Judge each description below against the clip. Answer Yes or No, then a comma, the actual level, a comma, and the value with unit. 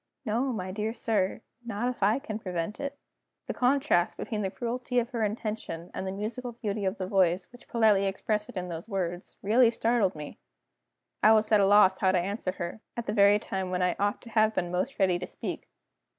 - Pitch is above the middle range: Yes, high, 210 Hz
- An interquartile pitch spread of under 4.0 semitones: Yes, average, 3.5 semitones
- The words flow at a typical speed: No, fast, 215 wpm